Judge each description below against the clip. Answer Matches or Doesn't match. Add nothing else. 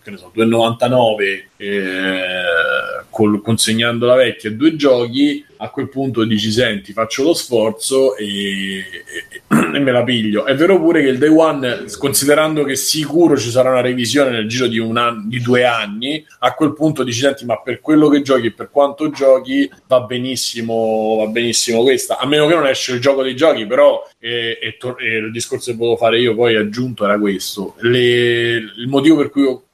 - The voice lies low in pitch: Matches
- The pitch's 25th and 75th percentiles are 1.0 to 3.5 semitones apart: Doesn't match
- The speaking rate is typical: Doesn't match